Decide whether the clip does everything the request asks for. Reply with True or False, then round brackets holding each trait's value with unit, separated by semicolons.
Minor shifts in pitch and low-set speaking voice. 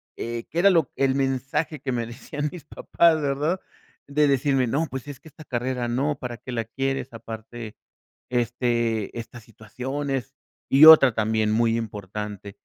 False (3.7 semitones; 125 Hz)